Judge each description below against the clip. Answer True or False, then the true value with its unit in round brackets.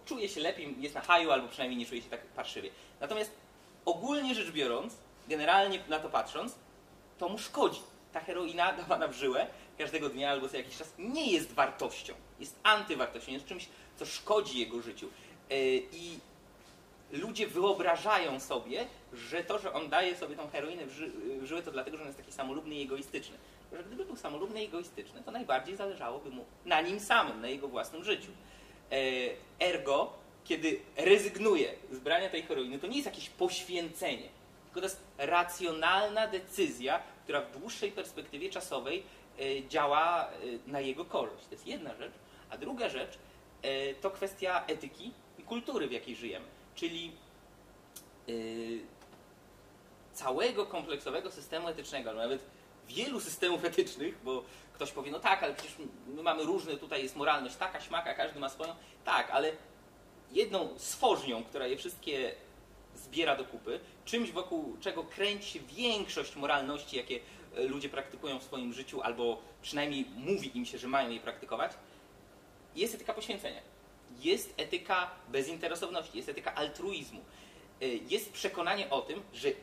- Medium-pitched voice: True (175 Hz)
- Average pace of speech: True (150 wpm)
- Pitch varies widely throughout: True (8.8 semitones)